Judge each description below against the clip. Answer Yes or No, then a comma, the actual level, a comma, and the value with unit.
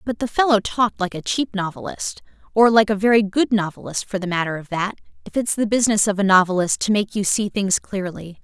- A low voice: No, high, 205 Hz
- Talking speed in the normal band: No, fast, 220 wpm